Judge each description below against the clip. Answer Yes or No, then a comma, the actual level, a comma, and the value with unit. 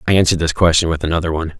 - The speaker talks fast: Yes, fast, 265 wpm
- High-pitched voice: No, very low, 80 Hz